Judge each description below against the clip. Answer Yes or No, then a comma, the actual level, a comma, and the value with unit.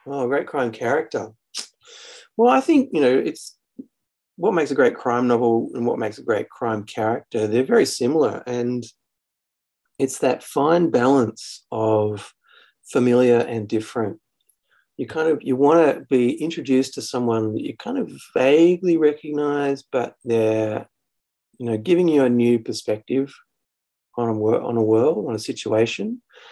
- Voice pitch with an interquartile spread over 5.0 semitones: Yes, wide, 5.6 semitones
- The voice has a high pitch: No, low, 125 Hz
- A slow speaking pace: No, average, 155 wpm